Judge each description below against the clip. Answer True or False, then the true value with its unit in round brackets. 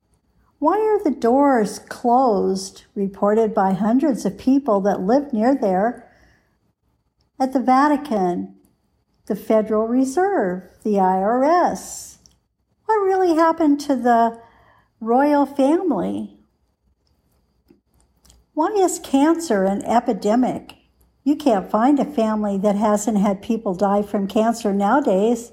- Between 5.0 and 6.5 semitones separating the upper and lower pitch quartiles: True (5.4 semitones)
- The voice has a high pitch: True (230 Hz)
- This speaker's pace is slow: True (110 wpm)